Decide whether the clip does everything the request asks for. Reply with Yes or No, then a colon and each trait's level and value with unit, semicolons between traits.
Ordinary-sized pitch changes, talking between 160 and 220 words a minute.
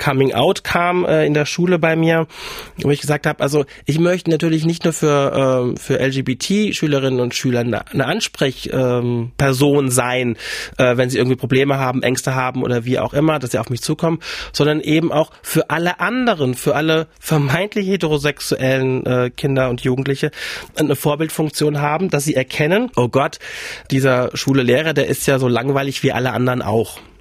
Yes: average, 3.5 semitones; average, 170 wpm